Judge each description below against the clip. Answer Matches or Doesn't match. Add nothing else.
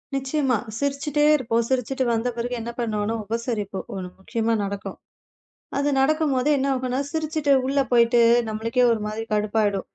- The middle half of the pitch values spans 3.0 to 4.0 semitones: Matches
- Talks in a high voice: Matches